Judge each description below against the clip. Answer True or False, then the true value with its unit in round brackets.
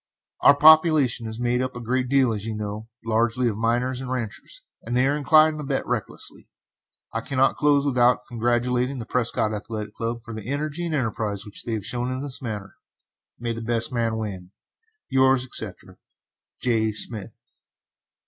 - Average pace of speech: True (170 wpm)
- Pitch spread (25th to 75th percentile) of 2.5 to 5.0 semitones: True (3.0 semitones)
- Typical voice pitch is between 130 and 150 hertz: False (120 Hz)